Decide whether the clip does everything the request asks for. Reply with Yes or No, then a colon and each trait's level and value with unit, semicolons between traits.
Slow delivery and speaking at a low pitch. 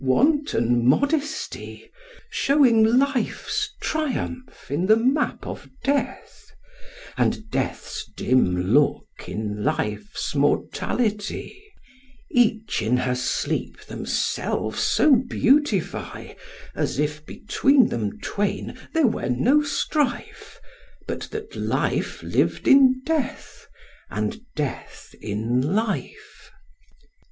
No: slow, 95 wpm; high, 225 Hz